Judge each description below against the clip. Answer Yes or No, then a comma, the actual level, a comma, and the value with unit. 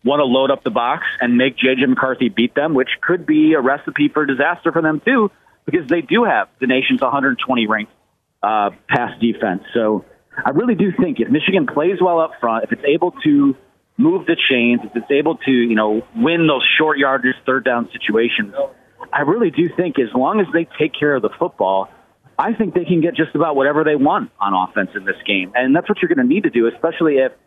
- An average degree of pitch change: No, wide, 5.7 semitones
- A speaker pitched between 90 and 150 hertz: Yes, medium, 140 Hz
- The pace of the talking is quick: Yes, fast, 225 wpm